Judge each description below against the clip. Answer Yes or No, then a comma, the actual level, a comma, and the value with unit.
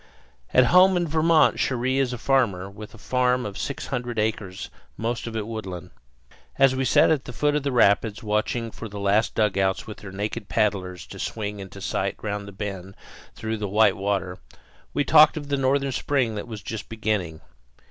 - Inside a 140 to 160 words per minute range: No, average, 195 wpm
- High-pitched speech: No, low, 110 Hz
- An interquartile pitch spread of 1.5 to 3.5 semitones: No, average, 4.3 semitones